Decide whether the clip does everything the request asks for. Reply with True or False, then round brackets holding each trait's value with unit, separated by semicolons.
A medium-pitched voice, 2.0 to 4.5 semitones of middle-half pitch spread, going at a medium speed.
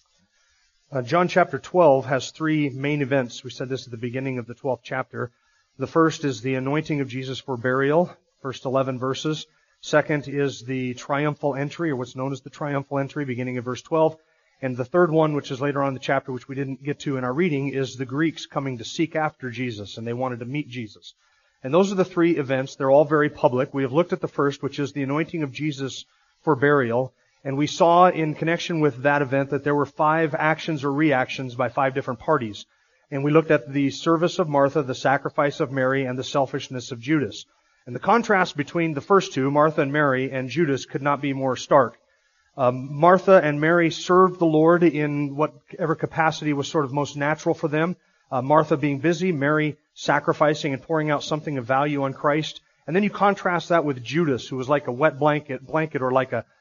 False (145 Hz; 3.1 semitones; 215 wpm)